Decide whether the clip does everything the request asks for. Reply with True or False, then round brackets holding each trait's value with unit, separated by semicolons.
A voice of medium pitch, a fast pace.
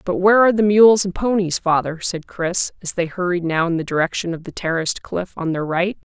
True (180 Hz; 235 wpm)